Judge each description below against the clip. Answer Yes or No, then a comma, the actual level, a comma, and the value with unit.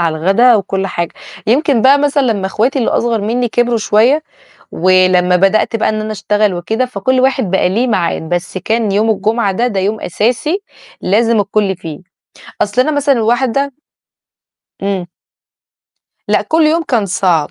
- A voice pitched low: No, high, 215 Hz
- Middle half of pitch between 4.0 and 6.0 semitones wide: Yes, average, 4.4 semitones